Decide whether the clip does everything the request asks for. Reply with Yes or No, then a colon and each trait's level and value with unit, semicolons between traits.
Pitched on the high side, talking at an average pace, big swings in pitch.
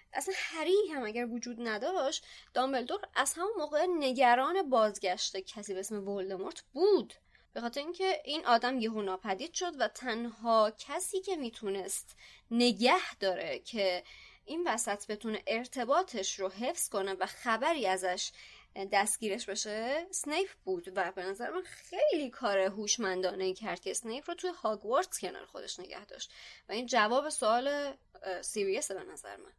Yes: high, 235 Hz; average, 145 wpm; wide, 7.4 semitones